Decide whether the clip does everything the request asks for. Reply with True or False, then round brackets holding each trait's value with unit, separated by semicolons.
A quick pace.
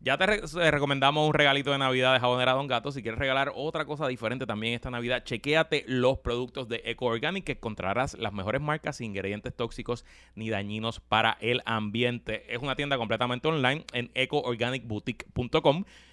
False (170 wpm)